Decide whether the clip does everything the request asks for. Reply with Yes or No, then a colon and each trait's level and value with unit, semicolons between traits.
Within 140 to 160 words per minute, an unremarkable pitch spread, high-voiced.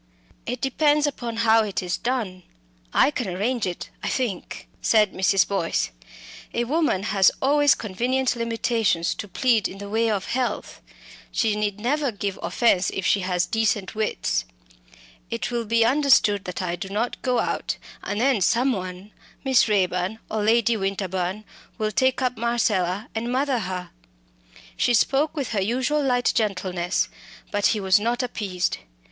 Yes: average, 155 wpm; average, 4.2 semitones; high, 220 Hz